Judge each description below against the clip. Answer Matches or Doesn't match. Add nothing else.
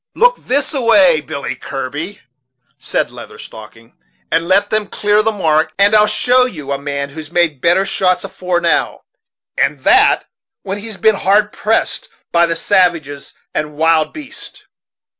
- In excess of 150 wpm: Matches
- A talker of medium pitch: Matches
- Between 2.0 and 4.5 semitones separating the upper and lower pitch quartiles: Doesn't match